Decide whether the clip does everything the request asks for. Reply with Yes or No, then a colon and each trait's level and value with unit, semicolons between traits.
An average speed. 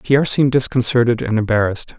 Yes: average, 150 wpm